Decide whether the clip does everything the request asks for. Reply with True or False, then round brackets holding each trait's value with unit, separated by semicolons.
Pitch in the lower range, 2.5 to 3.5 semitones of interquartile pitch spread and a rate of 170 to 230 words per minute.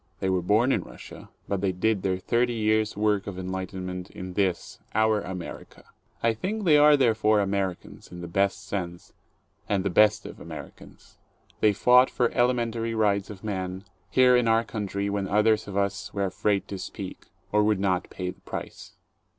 True (100 Hz; 2.9 semitones; 190 wpm)